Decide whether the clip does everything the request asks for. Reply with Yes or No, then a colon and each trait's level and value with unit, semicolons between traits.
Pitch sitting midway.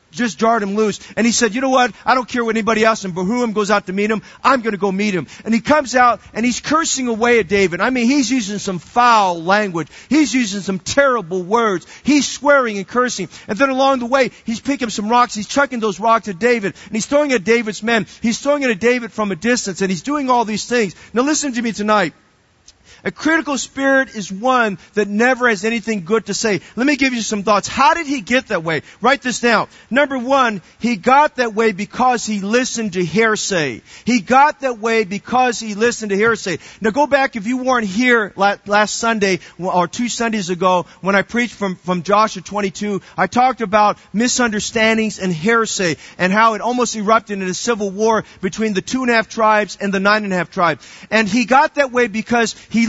No: high, 225 Hz